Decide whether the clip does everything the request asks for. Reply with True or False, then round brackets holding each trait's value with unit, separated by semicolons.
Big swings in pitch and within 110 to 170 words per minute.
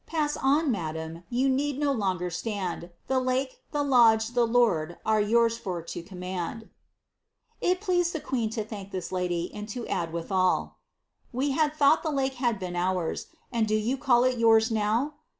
False (6.3 semitones; 185 wpm)